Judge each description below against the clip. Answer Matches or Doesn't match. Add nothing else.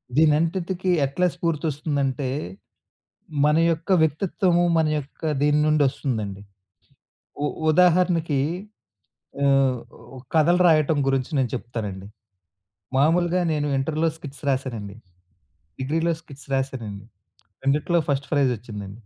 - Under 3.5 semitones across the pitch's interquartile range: Doesn't match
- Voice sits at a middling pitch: Matches